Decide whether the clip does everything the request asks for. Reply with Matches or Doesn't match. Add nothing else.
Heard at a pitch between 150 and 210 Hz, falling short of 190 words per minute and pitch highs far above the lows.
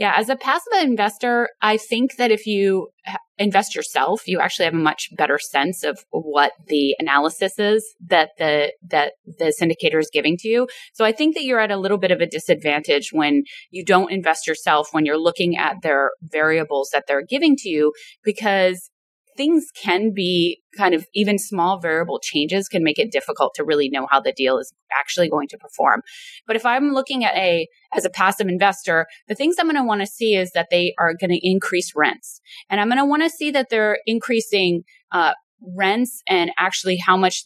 Doesn't match